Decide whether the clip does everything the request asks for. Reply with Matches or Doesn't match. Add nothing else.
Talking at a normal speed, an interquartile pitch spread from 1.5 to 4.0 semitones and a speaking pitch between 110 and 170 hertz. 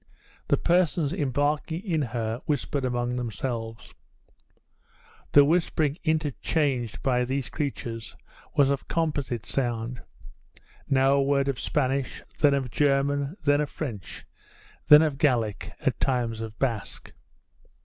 Doesn't match